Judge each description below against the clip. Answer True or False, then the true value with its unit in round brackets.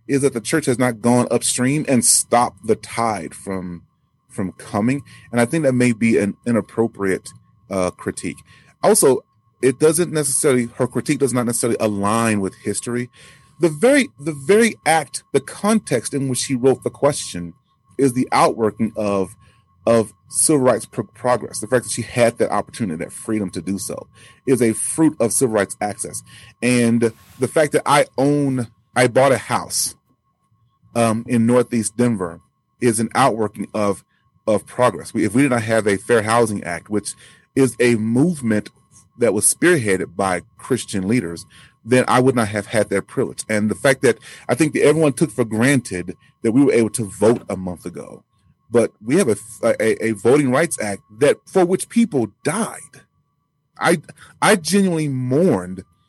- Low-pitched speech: True (120 Hz)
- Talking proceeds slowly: False (175 wpm)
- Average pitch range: True (4.1 semitones)